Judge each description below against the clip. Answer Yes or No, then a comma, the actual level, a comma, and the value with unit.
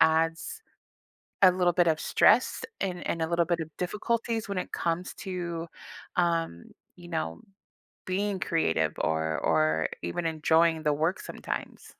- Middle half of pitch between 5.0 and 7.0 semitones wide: No, narrow, 2.5 semitones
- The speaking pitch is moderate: Yes, medium, 170 Hz